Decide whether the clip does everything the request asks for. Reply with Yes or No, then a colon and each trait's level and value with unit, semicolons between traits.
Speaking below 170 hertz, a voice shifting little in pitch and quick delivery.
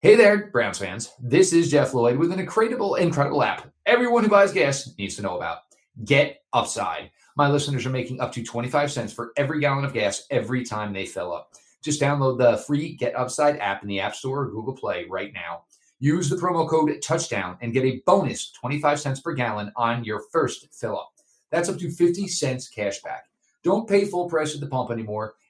No: medium, 140 Hz; wide, 5.4 semitones; fast, 210 wpm